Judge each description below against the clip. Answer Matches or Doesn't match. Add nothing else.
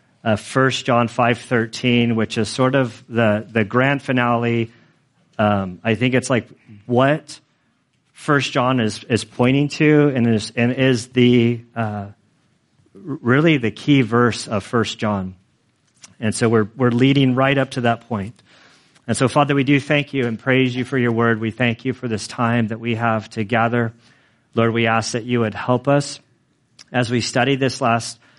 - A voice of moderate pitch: Doesn't match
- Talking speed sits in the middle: Matches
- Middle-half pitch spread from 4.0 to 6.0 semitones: Doesn't match